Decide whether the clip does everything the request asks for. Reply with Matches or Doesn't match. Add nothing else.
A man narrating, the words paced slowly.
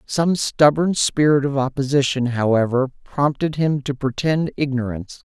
Matches